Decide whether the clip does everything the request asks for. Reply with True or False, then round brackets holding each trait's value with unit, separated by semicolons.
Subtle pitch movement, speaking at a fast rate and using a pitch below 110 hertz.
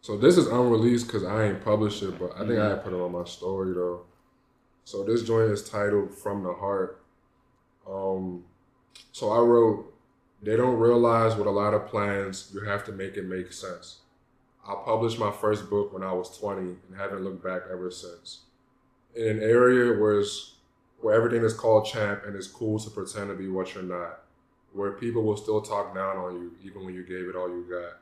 False (3.3 semitones; 210 wpm; 100 Hz)